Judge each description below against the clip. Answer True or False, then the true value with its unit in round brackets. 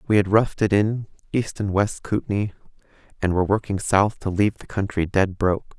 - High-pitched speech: False (100 Hz)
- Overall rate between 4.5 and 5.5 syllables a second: False (5.8 syllables/s)